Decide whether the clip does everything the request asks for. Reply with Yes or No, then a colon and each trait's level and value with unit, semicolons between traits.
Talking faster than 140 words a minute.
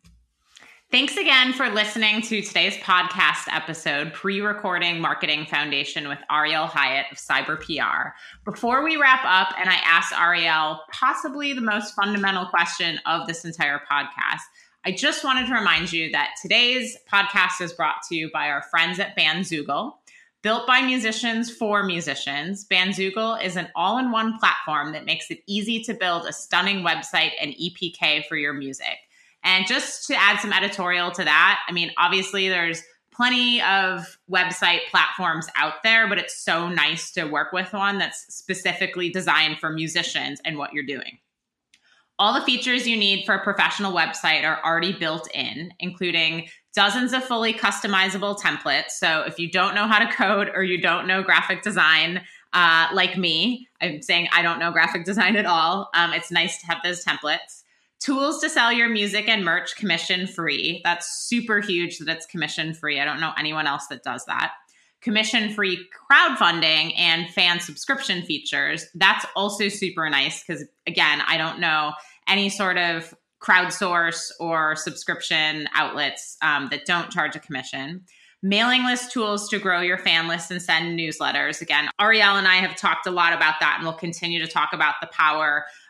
Yes: average, 170 wpm